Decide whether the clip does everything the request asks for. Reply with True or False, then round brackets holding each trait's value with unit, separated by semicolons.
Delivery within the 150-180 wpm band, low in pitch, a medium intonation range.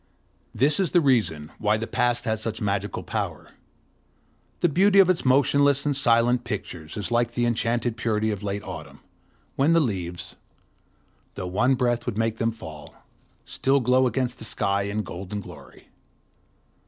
True (160 wpm; 115 Hz; 4.2 semitones)